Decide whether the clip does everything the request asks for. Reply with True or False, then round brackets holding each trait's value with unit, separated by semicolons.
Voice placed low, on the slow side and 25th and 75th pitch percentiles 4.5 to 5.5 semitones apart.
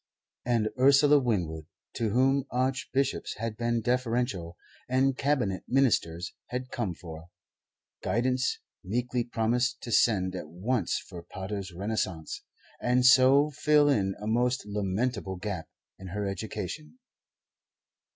True (115 Hz; 120 wpm; 5.1 semitones)